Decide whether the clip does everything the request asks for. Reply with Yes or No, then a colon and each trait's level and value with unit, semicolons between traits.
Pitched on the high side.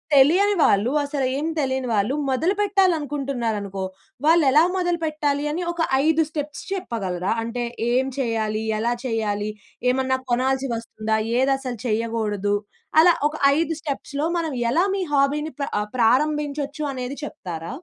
Yes: very high, 270 Hz